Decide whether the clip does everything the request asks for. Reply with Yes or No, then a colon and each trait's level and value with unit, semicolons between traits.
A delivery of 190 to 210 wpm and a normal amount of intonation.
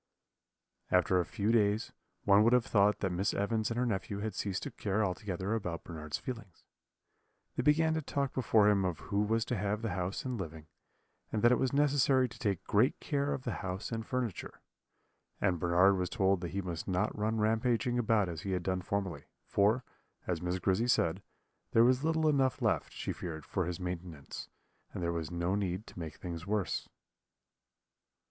Yes: average, 195 wpm; average, 4.4 semitones